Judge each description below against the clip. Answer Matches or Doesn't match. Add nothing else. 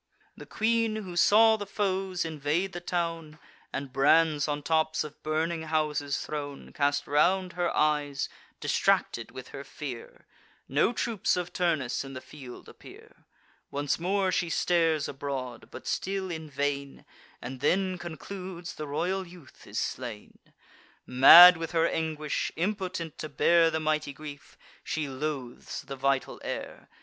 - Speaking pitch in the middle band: Matches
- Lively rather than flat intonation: Doesn't match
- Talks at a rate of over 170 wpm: Doesn't match